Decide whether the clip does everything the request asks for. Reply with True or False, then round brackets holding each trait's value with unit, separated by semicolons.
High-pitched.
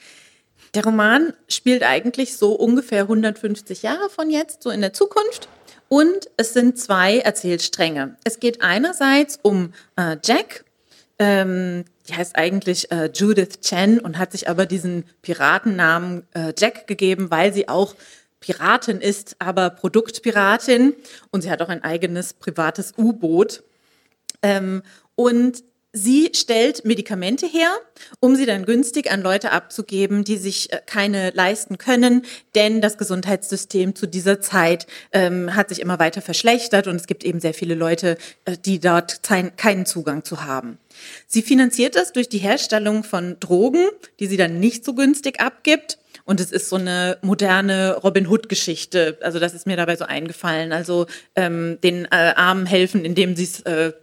True (195 Hz)